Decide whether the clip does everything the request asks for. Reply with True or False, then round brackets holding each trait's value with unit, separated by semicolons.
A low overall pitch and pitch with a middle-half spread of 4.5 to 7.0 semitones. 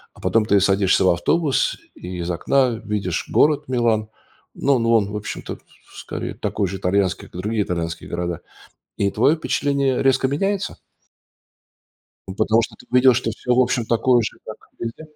True (110 Hz; 5.1 semitones)